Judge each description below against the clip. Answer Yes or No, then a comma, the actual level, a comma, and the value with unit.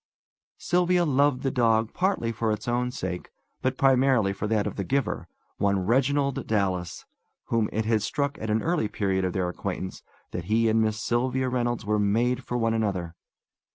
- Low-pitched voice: Yes, low, 115 Hz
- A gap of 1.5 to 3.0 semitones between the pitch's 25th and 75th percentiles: No, average, 4.0 semitones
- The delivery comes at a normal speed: Yes, average, 180 wpm